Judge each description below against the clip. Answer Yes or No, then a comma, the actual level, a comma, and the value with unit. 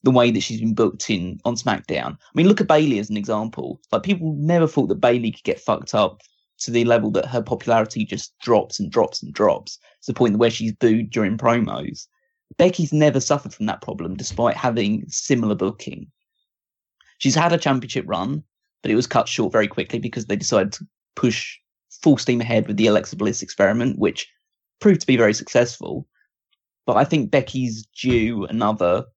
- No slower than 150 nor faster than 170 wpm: No, average, 195 wpm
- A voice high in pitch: No, low, 120 Hz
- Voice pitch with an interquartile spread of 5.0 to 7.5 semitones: Yes, wide, 5.4 semitones